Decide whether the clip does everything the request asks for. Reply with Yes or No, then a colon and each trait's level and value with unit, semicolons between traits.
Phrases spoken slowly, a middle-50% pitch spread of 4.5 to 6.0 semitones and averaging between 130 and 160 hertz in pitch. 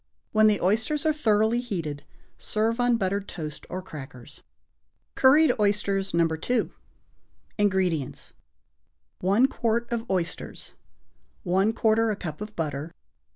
No: slow, 115 wpm; average, 4.8 semitones; high, 205 Hz